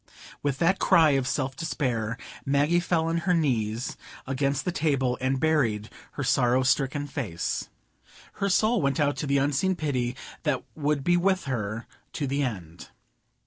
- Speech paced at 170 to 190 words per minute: No, average, 160 wpm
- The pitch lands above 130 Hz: Yes, medium, 140 Hz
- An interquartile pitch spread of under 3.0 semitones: No, average, 4.1 semitones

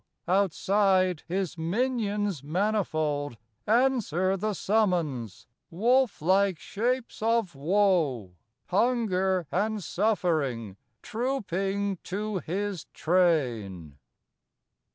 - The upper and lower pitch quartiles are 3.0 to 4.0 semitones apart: No, average, 4.7 semitones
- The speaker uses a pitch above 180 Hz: Yes, high, 190 Hz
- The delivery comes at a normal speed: No, slow, 75 wpm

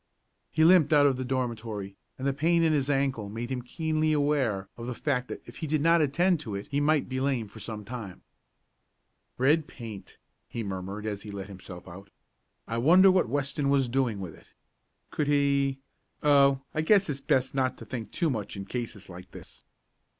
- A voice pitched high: No, low, 130 Hz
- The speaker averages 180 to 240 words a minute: Yes, average, 200 wpm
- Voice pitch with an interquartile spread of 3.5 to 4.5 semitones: No, average, 5.2 semitones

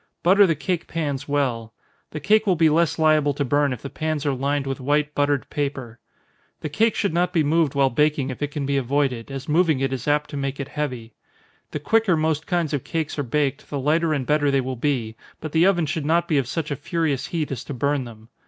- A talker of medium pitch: Yes, medium, 145 Hz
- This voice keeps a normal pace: No, fast, 240 wpm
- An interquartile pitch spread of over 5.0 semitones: No, average, 2.8 semitones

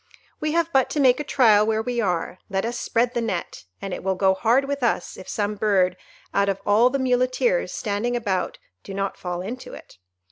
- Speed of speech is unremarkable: No, fast, 215 wpm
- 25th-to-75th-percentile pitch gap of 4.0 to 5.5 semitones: Yes, average, 4.5 semitones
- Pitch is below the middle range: No, high, 220 Hz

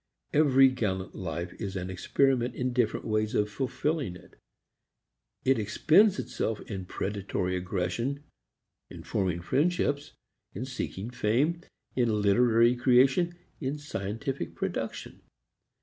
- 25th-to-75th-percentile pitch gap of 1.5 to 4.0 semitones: No, wide, 5.5 semitones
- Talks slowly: Yes, slow, 115 wpm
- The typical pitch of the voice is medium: No, low, 120 Hz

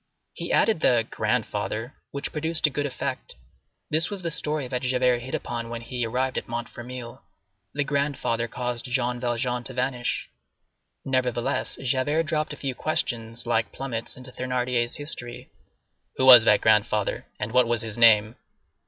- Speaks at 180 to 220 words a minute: No, average, 155 wpm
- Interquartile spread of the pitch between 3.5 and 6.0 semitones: No, narrow, 2.5 semitones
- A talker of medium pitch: No, low, 125 Hz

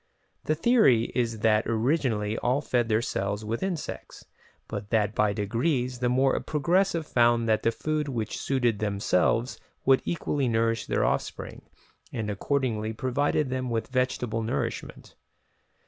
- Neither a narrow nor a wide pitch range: Yes, average, 3.7 semitones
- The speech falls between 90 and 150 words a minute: Yes, average, 140 wpm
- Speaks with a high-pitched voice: No, low, 120 Hz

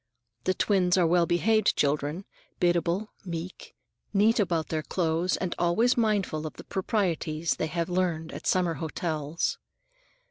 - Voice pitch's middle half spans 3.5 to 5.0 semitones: No, average, 2.9 semitones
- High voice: No, medium, 175 Hz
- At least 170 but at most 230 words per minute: No, average, 140 wpm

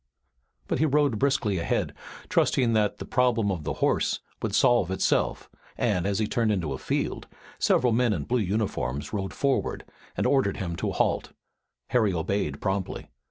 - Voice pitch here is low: Yes, low, 105 Hz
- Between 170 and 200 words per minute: No, average, 160 wpm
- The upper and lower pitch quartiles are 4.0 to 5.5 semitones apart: Yes, average, 4.8 semitones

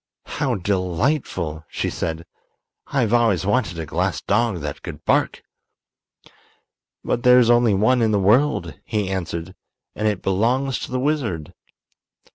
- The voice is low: Yes, low, 105 Hz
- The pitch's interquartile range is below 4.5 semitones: No, average, 5.3 semitones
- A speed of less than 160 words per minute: Yes, average, 140 wpm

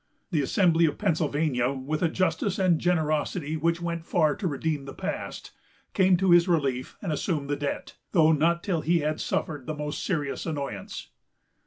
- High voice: No, medium, 160 Hz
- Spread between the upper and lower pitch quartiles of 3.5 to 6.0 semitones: No, average, 2.7 semitones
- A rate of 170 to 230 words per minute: Yes, average, 180 wpm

